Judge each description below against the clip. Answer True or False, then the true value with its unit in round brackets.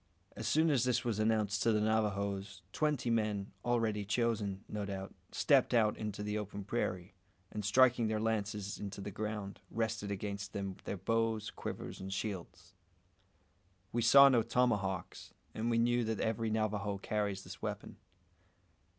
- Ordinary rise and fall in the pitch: False (2.2 semitones)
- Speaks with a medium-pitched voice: False (105 Hz)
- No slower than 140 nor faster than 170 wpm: True (155 wpm)